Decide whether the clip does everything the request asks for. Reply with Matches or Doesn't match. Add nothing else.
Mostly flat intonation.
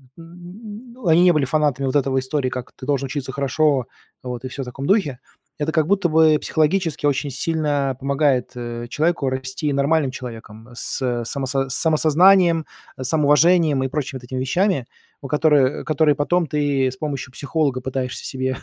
Doesn't match